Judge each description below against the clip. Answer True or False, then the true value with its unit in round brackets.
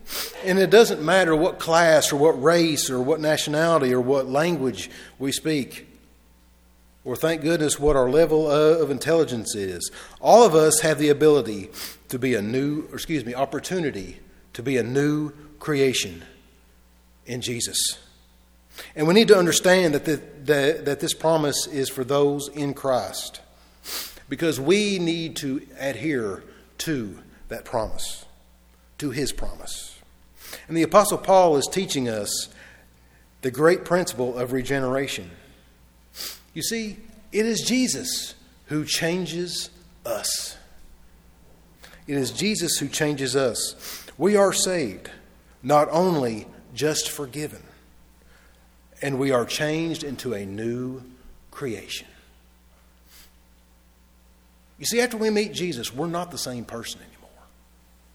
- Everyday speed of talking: False (130 wpm)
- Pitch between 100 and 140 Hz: True (135 Hz)